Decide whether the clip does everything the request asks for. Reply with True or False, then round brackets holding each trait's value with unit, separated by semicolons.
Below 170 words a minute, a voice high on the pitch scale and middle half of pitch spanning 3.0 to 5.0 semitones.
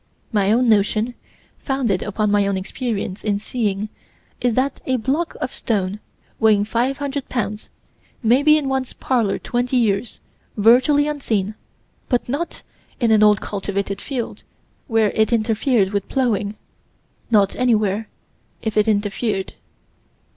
True (135 wpm; 220 Hz; 3.7 semitones)